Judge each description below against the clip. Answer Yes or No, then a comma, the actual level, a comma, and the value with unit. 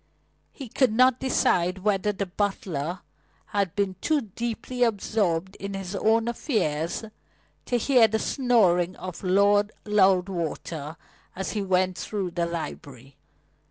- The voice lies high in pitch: Yes, high, 195 Hz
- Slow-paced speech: Yes, slow, 125 wpm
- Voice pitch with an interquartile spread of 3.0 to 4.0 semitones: Yes, average, 3.7 semitones